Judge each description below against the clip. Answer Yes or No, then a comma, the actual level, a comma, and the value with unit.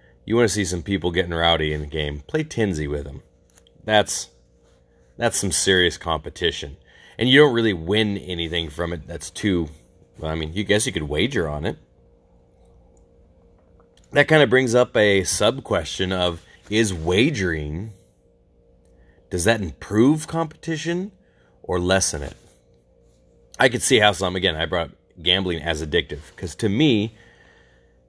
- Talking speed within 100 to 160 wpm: Yes, average, 150 wpm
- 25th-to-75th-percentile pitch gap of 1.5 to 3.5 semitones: No, average, 5.0 semitones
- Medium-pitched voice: No, very low, 90 Hz